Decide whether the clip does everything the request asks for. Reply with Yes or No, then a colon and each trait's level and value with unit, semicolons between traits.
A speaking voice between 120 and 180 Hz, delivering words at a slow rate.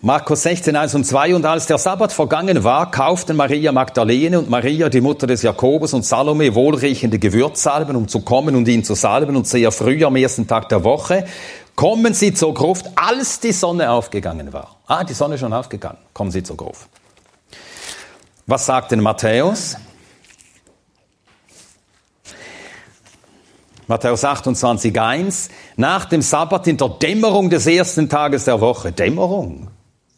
No: medium, 140 Hz; average, 155 wpm